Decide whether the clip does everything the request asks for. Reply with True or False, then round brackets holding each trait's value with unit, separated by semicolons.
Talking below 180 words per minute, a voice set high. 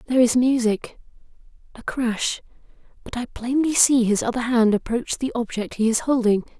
True (145 wpm; 240 Hz)